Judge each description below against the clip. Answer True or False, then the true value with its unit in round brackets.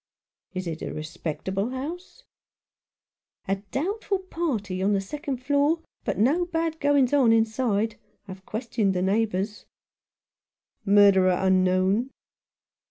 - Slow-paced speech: True (125 wpm)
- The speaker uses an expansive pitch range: True (7.0 semitones)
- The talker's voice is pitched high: True (220 Hz)